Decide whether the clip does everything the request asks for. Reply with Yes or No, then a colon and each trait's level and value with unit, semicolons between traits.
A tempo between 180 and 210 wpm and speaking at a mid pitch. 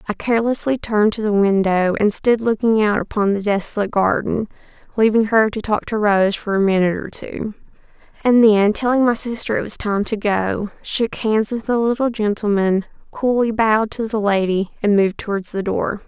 No: average, 190 wpm; high, 210 Hz